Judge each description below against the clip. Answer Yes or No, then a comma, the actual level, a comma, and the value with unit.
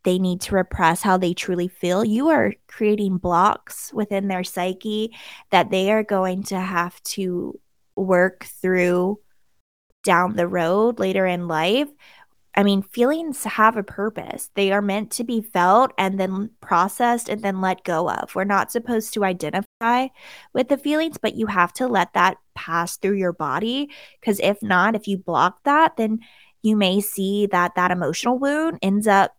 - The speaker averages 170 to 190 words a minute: Yes, average, 175 wpm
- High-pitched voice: Yes, high, 195 Hz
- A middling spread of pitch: Yes, average, 3.6 semitones